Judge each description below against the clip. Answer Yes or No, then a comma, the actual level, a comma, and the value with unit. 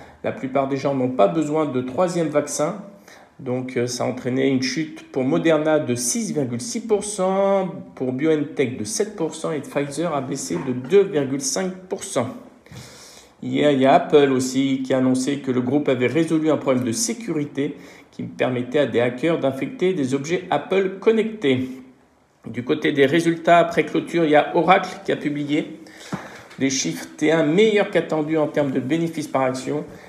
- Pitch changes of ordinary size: Yes, average, 3.9 semitones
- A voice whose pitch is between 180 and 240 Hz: No, medium, 150 Hz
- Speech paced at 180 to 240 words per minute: No, average, 165 wpm